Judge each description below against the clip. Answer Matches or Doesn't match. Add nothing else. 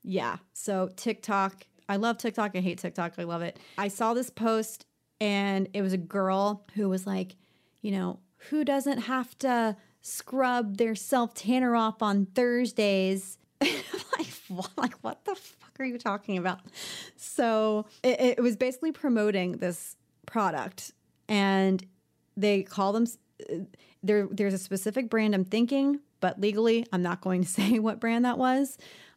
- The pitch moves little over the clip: Doesn't match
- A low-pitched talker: Doesn't match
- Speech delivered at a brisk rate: Doesn't match